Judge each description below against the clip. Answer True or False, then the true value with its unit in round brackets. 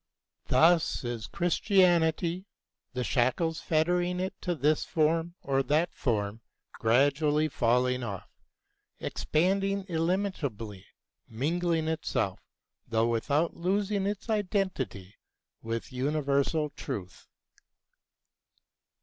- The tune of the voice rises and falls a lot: True (5.9 semitones)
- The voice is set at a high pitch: False (155 Hz)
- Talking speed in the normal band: False (90 wpm)